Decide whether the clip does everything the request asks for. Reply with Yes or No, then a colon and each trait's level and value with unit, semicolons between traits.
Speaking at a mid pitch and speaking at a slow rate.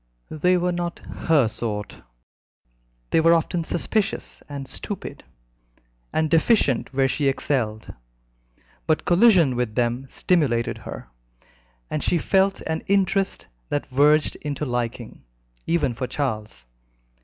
Yes: medium, 150 Hz; slow, 120 wpm